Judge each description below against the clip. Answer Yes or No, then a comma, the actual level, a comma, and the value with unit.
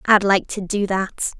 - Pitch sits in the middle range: No, high, 195 Hz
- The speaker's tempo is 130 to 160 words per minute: No, fast, 215 wpm